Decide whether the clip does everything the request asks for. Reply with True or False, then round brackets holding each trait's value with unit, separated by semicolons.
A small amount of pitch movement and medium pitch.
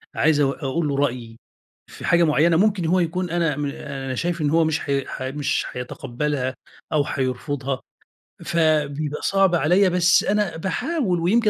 False (4.0 semitones; 155 Hz)